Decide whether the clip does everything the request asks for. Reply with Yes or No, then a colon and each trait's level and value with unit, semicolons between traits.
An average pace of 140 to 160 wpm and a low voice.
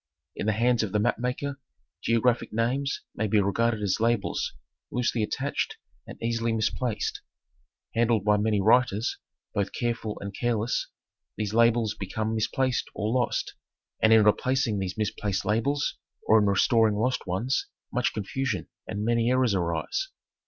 Yes: average, 145 wpm; low, 115 Hz